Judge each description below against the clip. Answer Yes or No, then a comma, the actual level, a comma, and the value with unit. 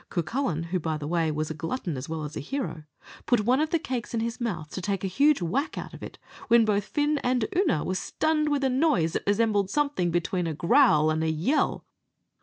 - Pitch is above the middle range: Yes, high, 200 Hz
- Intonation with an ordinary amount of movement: No, wide, 8.6 semitones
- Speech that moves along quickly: Yes, fast, 230 wpm